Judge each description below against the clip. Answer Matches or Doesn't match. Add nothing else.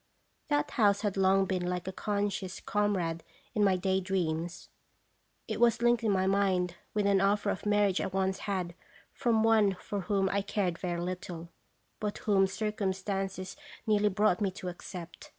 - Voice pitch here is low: Doesn't match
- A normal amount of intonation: Doesn't match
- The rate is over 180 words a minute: Doesn't match